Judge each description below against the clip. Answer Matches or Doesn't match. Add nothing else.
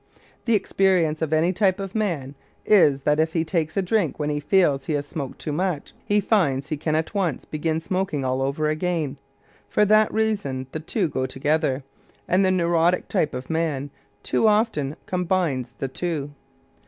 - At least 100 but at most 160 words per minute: Doesn't match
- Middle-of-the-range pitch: Matches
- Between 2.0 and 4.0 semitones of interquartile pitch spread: Doesn't match